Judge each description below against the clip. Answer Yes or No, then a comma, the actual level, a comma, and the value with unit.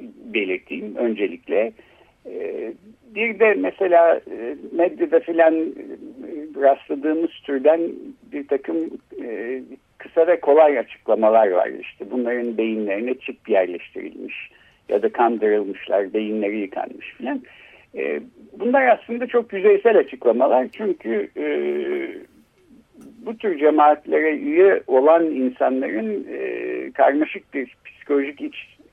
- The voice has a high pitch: Yes, high, 205 Hz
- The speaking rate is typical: No, slow, 90 wpm